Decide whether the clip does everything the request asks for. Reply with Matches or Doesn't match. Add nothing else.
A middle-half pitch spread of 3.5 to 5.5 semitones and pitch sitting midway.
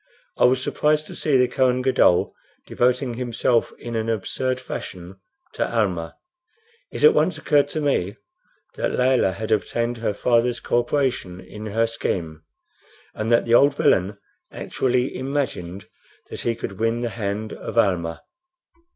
Doesn't match